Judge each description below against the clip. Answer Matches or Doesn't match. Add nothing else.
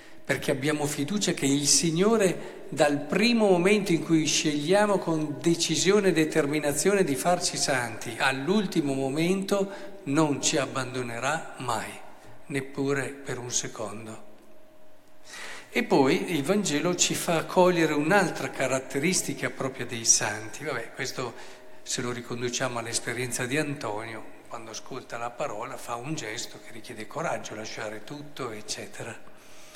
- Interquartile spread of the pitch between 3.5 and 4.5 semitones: Doesn't match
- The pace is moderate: Matches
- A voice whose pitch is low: Doesn't match